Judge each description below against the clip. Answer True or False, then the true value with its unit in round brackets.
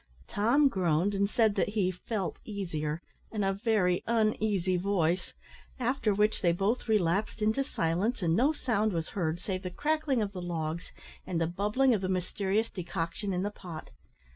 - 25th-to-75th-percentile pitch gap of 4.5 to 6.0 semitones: False (3.6 semitones)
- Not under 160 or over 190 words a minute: True (170 wpm)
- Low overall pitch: False (195 Hz)